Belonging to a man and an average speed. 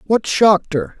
Yes: male; average, 180 wpm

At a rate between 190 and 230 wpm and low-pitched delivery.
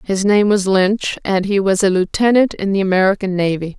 No: fast, 205 wpm; high, 195 Hz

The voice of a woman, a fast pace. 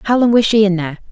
Yes: female; fast, 320 wpm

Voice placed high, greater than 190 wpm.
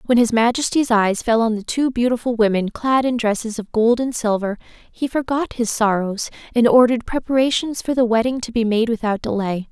Yes: high, 230 Hz; average, 200 wpm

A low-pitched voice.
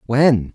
Yes: low, 120 Hz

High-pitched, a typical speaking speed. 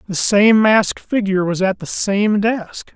Yes: high, 205 Hz; average, 185 wpm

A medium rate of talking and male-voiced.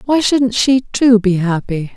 No: average, 185 wpm; female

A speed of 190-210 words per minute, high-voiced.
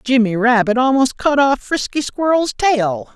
No: average, 150 wpm; very high, 255 Hz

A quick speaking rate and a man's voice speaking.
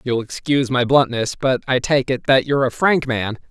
Yes: fast, 225 wpm; male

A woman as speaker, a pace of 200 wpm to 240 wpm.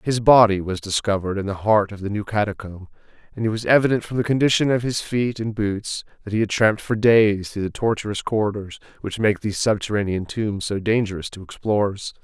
No: male; fast, 205 wpm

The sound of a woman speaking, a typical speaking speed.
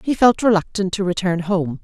Yes: female; average, 195 wpm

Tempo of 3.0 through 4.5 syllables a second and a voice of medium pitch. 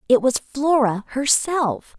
No: 3.6 syllables/s; very high, 265 Hz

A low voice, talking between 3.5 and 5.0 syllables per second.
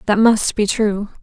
No: high, 210 Hz; 4.1 syllables/s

